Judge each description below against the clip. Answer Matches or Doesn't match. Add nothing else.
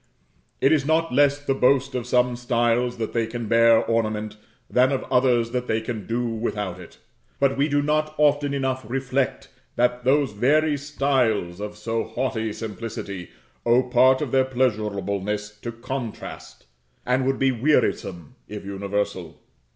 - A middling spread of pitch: Matches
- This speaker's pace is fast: Doesn't match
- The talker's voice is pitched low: Matches